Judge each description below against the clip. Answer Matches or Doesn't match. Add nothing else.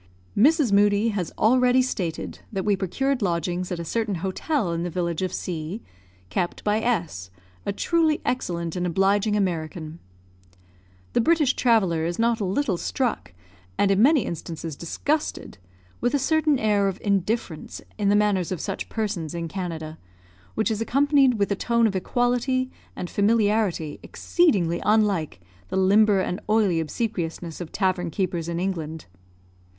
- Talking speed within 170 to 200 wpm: Doesn't match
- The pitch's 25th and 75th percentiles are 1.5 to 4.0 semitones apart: Doesn't match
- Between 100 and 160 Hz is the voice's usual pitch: Doesn't match